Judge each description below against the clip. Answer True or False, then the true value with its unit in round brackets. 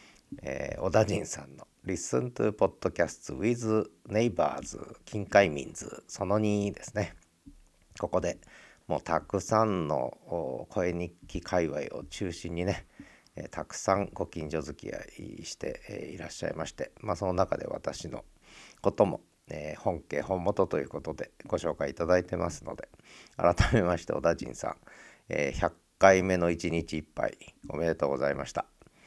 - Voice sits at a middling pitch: False (90 Hz)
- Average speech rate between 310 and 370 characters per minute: True (330 characters per minute)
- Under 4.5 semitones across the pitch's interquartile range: True (3.5 semitones)